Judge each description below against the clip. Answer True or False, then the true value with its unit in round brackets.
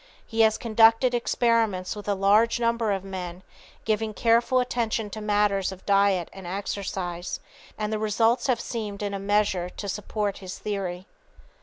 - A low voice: False (210 Hz)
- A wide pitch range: False (2.6 semitones)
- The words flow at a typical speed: True (160 wpm)